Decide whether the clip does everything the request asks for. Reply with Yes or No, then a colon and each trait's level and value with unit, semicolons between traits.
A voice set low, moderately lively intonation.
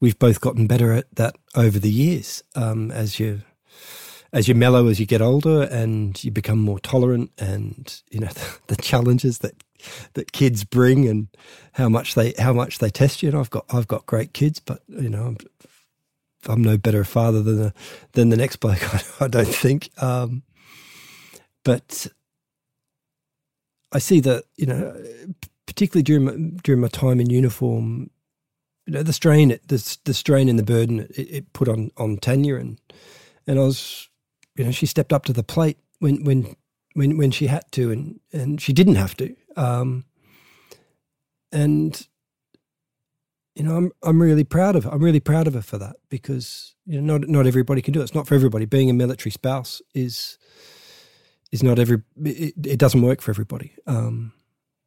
Yes: low, 130 Hz; average, 4.2 semitones